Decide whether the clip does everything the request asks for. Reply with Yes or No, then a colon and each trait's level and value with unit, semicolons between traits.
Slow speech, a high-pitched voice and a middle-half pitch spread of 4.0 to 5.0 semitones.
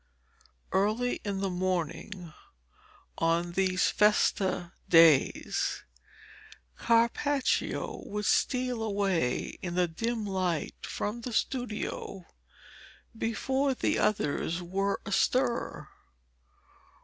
Yes: slow, 85 wpm; high, 200 Hz; average, 4.5 semitones